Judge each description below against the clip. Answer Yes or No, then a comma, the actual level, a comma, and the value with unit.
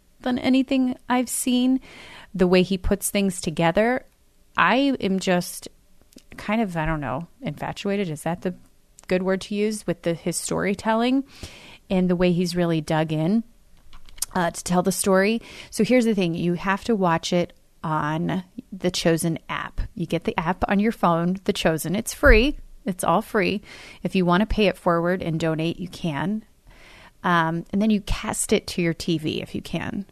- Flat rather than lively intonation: No, average, 3.8 semitones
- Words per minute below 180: No, average, 185 wpm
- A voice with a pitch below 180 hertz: No, medium, 185 Hz